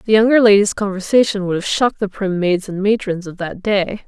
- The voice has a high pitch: Yes, high, 200 Hz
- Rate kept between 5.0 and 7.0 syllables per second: Yes, 5.5 syllables/s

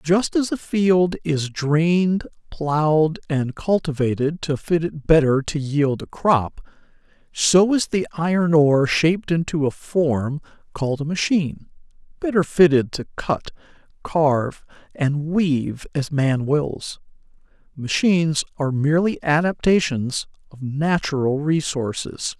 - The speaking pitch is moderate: Yes, medium, 155 Hz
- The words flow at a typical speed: No, slow, 125 wpm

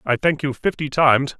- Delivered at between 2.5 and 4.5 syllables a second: No, 5.5 syllables/s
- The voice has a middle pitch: Yes, medium, 145 Hz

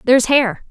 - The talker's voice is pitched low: No, very high, 250 Hz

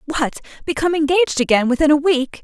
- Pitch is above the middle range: Yes, very high, 295 Hz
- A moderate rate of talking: Yes, average, 175 wpm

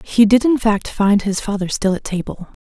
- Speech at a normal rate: No, fast, 230 wpm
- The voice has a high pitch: Yes, high, 210 Hz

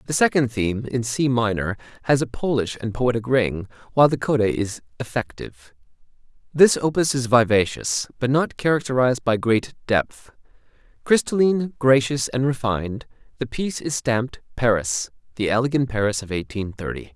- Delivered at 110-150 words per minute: Yes, average, 145 wpm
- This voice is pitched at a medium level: No, low, 120 Hz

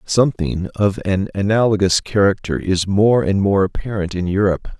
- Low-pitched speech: Yes, low, 100 Hz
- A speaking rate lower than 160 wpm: Yes, average, 150 wpm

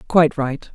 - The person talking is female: Yes, female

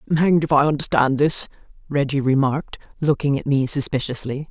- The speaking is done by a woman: Yes, female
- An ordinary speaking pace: Yes, average, 160 wpm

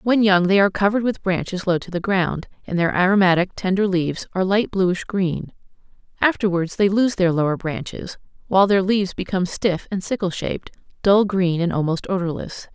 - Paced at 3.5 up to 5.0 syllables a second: No, 5.6 syllables/s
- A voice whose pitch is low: No, high, 190 Hz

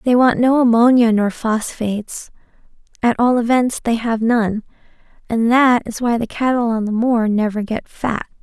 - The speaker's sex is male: No, female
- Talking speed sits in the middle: Yes, average, 165 wpm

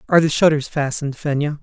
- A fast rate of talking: No, average, 185 wpm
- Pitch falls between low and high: Yes, medium, 150 Hz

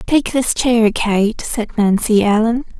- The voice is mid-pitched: No, high, 225 Hz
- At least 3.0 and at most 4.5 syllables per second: Yes, 3.6 syllables/s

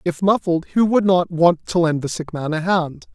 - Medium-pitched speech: Yes, medium, 175 Hz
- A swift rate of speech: Yes, fast, 250 wpm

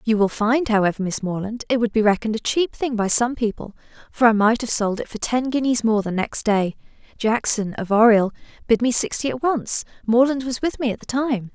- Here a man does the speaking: No, female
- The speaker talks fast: Yes, fast, 230 wpm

